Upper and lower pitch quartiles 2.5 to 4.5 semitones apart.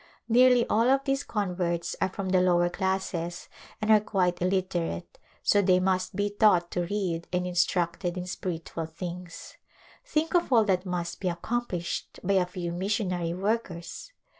Yes: average, 2.8 semitones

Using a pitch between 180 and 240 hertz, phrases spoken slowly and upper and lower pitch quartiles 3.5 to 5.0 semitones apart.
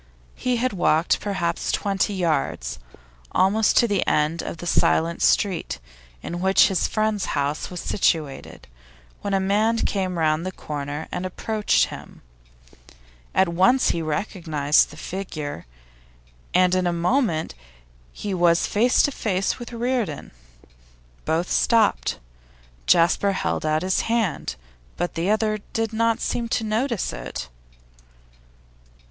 Yes: medium, 185 Hz; slow, 130 wpm; average, 4.6 semitones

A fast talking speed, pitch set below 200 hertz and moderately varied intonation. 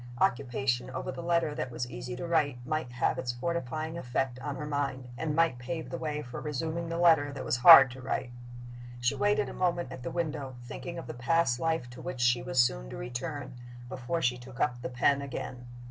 Yes: fast, 215 wpm; low, 135 Hz; average, 4.7 semitones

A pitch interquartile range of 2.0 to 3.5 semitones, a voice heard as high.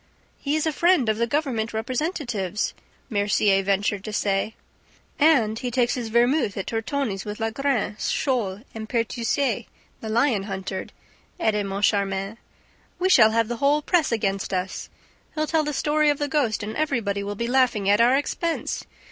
No: wide, 5.5 semitones; high, 230 Hz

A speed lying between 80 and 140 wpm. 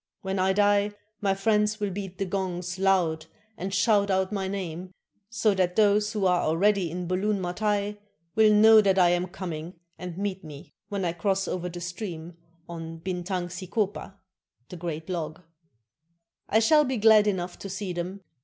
No: average, 175 wpm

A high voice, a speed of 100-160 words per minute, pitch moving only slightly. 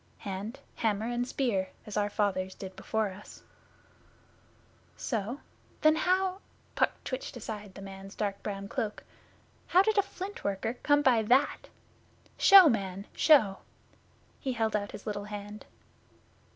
No: high, 215 Hz; average, 140 wpm; average, 4.9 semitones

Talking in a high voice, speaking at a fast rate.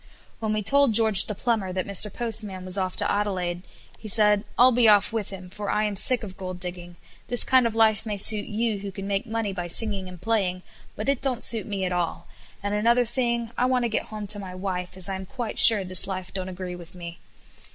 Yes: high, 205 Hz; fast, 240 wpm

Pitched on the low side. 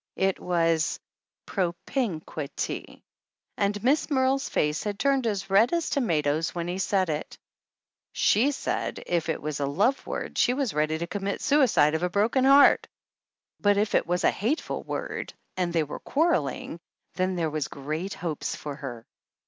No: medium, 185 Hz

